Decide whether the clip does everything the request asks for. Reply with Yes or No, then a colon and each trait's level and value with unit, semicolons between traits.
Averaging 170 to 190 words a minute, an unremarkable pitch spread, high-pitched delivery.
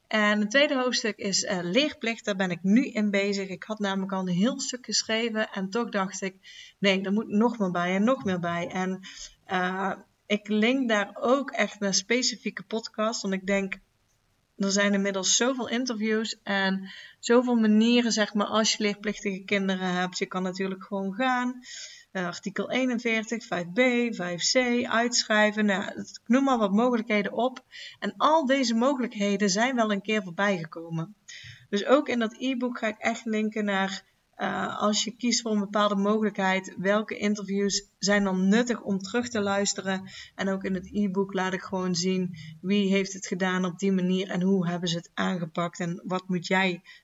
Yes: average, 185 wpm; average, 3.0 semitones; high, 205 Hz